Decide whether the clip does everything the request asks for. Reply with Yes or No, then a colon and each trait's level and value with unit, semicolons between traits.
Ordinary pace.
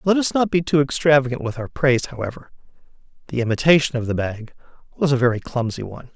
Yes: average, 195 wpm